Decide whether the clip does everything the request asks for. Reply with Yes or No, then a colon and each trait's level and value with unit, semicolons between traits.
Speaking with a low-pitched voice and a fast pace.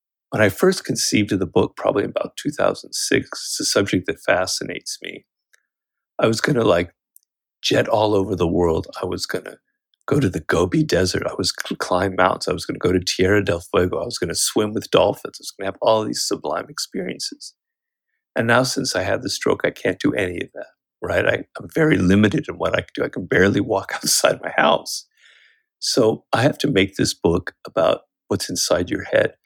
Yes: low, 110 Hz; fast, 220 wpm